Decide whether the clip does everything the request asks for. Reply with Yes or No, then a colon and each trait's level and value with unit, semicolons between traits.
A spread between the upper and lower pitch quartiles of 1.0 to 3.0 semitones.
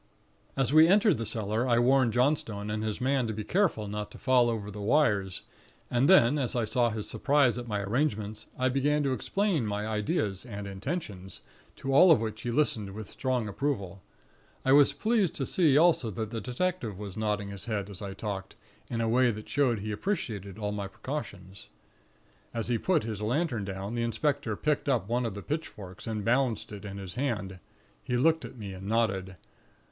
No: average, 4.8 semitones